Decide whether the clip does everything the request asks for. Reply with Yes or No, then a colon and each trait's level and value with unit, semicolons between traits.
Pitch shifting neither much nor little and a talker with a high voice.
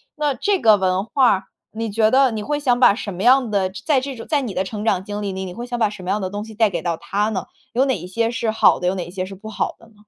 Yes: average, 4.2 semitones; high, 215 Hz